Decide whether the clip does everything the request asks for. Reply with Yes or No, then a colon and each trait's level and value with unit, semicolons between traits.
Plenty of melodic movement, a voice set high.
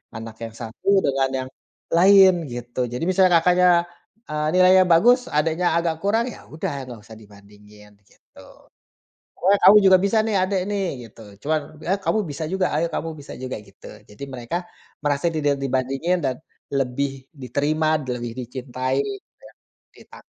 No: wide, 6.7 semitones; medium, 145 Hz